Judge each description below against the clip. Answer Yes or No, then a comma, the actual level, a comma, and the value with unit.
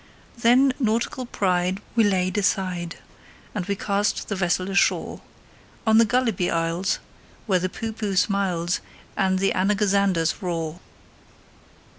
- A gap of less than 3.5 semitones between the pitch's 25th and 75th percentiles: Yes, average, 2.9 semitones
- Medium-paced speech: No, slow, 120 wpm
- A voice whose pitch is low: No, high, 195 Hz